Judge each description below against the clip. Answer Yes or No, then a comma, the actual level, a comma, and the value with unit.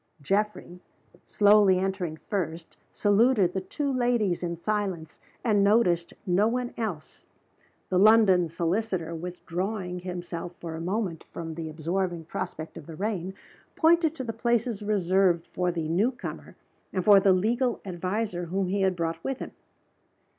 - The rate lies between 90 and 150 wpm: Yes, average, 145 wpm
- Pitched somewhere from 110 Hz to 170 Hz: No, high, 190 Hz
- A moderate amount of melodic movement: Yes, average, 3.8 semitones